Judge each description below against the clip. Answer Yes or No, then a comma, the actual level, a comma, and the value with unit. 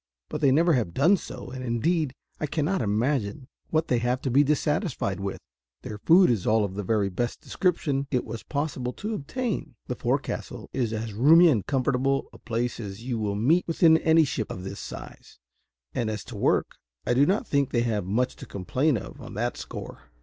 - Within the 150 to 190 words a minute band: No, fast, 205 wpm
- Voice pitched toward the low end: Yes, low, 130 Hz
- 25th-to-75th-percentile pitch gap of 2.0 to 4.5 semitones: No, wide, 5.5 semitones